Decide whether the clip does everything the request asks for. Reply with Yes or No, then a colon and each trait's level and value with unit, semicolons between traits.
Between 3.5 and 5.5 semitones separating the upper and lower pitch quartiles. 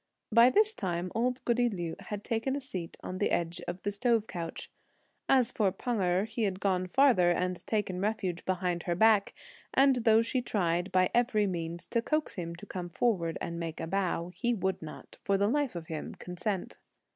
Yes: average, 4.7 semitones